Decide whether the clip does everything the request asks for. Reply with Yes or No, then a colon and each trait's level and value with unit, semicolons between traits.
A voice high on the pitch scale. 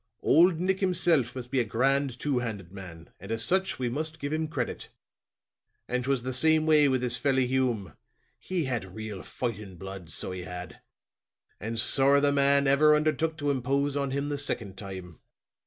No: low, 130 Hz